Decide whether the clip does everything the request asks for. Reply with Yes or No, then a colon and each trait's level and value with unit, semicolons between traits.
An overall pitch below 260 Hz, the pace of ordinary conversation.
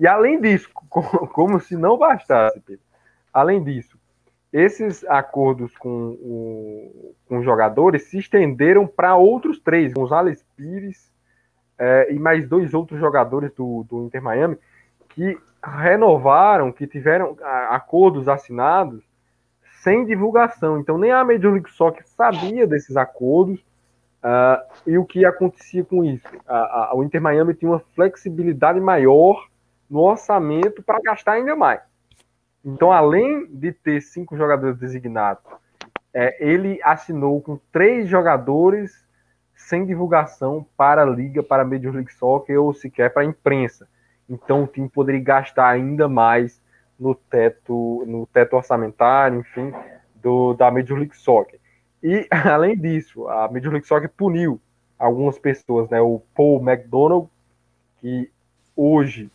Yes: medium, 140 Hz; average, 135 wpm